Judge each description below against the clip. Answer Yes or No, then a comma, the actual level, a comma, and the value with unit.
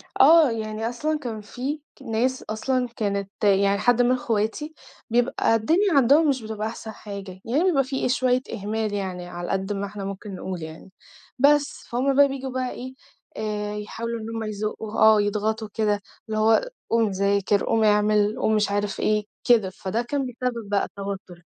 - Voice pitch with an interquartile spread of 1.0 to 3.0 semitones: No, average, 3.7 semitones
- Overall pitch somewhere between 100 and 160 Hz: No, high, 220 Hz